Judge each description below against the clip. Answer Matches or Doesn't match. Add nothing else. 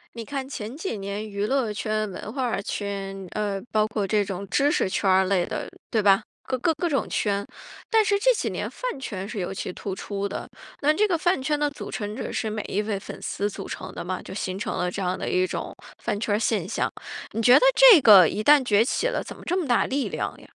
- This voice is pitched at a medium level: Doesn't match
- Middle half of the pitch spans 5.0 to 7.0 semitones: Matches